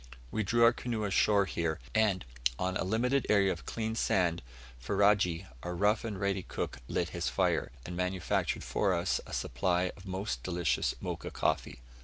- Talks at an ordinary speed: Yes, average, 170 wpm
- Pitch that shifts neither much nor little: Yes, average, 3.2 semitones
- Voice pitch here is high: No, very low, 95 Hz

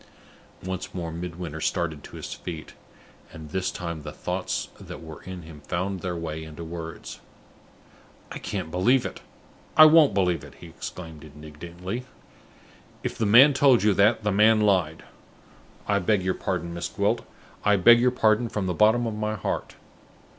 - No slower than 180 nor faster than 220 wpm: No, average, 170 wpm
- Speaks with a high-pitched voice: No, very low, 90 Hz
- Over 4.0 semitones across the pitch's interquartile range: Yes, average, 4.5 semitones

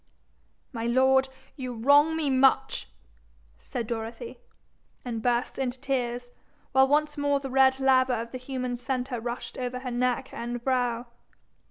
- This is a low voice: No, very high, 255 Hz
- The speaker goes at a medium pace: Yes, average, 145 wpm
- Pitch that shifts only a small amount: Yes, narrow, 1.7 semitones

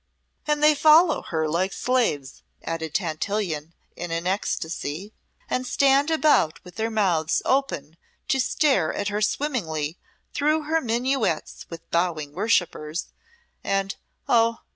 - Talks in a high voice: Yes, high, 200 Hz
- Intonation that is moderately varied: No, wide, 8.4 semitones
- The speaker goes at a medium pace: No, slow, 125 wpm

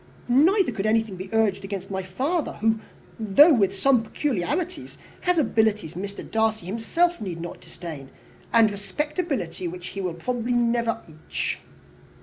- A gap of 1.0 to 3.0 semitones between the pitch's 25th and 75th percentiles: No, average, 4.9 semitones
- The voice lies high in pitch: Yes, high, 220 Hz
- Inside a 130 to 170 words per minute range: Yes, average, 145 wpm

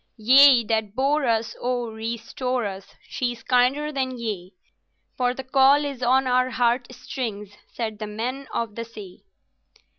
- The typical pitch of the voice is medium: No, high, 245 Hz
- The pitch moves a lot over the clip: No, average, 2.8 semitones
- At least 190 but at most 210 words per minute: No, average, 155 wpm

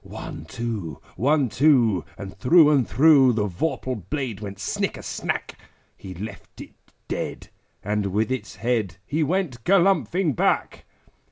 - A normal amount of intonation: No, wide, 6.7 semitones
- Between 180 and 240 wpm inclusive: No, average, 140 wpm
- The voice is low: Yes, low, 120 Hz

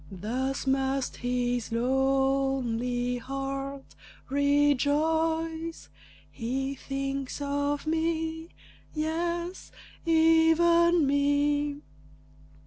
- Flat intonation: No, average, 3.2 semitones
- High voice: Yes, very high, 280 Hz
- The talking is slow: Yes, slow, 60 wpm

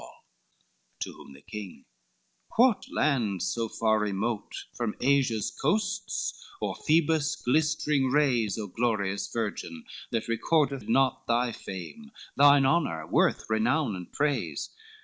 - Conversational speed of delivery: No, slow, 125 wpm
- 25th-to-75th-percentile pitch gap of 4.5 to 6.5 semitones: Yes, wide, 5.6 semitones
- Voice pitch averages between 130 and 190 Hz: No, low, 120 Hz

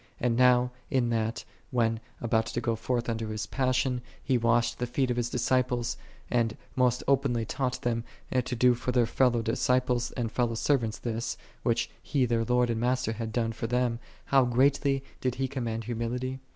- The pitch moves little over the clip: Yes, narrow, 1.7 semitones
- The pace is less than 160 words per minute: No, average, 180 wpm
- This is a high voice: No, low, 120 Hz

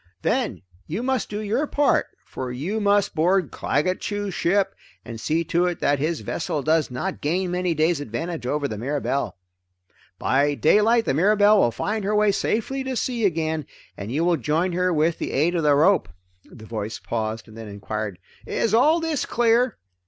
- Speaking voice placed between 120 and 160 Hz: No, medium, 170 Hz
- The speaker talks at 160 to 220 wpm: Yes, average, 185 wpm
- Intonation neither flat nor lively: No, wide, 6.4 semitones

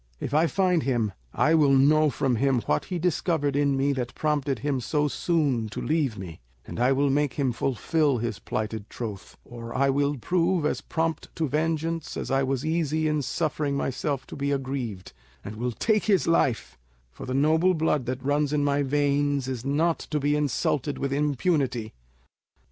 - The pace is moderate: Yes, average, 185 wpm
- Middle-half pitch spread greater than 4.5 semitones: No, average, 3.1 semitones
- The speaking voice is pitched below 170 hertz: Yes, medium, 140 Hz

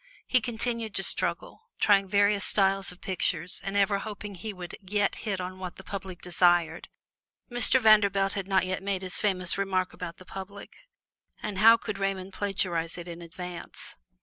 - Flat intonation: Yes, narrow, 1.9 semitones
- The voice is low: No, high, 195 Hz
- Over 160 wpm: Yes, average, 175 wpm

